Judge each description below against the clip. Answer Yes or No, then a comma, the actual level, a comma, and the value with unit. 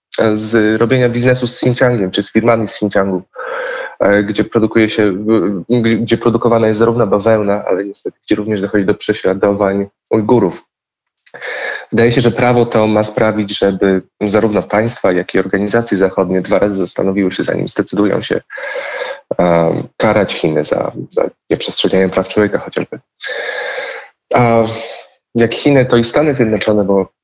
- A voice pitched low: Yes, low, 110 Hz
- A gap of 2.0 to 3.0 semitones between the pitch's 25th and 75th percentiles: Yes, narrow, 2.6 semitones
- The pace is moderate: Yes, average, 140 wpm